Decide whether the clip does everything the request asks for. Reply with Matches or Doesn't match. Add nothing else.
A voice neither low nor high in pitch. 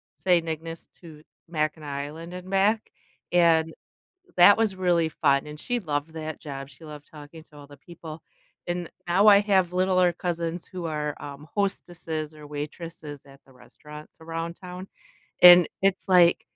Matches